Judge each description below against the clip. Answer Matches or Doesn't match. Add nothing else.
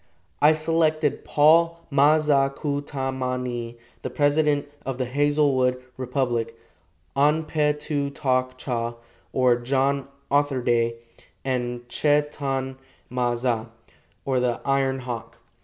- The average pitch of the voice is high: Doesn't match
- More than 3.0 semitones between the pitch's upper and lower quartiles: Doesn't match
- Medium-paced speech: Doesn't match